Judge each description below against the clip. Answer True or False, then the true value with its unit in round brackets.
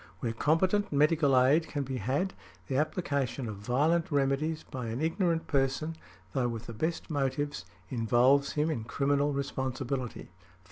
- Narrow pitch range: False (3.5 semitones)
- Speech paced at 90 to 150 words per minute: True (145 wpm)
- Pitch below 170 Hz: True (140 Hz)